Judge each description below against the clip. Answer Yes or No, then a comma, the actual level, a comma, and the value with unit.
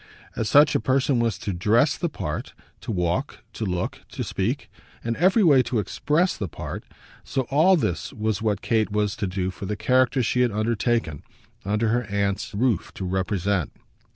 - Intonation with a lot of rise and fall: No, average, 4.4 semitones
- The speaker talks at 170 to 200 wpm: Yes, average, 180 wpm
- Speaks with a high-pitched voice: No, low, 110 Hz